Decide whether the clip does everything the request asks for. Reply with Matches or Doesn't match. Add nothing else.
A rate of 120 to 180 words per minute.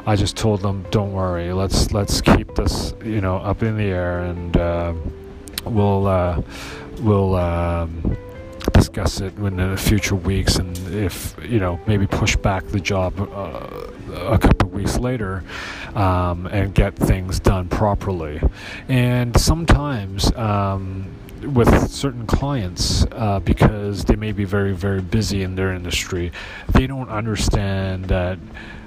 Matches